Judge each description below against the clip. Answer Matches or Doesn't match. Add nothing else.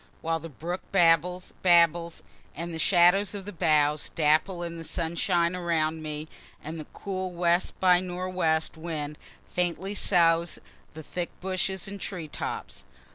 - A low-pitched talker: Doesn't match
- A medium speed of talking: Matches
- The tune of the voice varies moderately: Doesn't match